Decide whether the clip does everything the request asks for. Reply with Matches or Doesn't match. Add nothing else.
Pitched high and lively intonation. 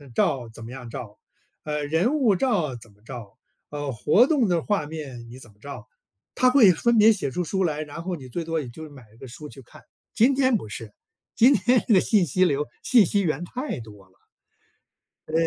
Doesn't match